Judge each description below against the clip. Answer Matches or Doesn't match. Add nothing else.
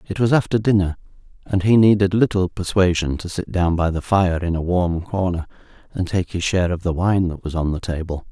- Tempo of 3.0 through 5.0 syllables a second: Doesn't match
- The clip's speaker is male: Matches